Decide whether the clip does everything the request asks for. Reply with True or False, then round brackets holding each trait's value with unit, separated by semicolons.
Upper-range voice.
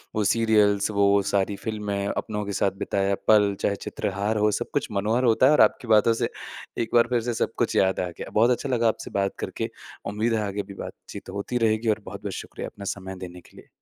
False (105 Hz)